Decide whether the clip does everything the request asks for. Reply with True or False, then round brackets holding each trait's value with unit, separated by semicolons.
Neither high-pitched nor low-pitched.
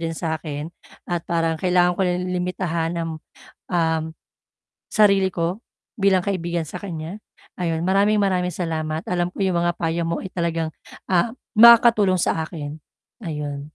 True (175 Hz)